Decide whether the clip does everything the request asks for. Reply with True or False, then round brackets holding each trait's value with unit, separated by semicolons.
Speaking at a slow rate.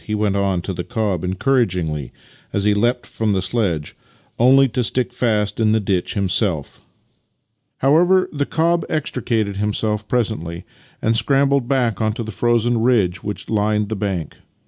False (165 wpm)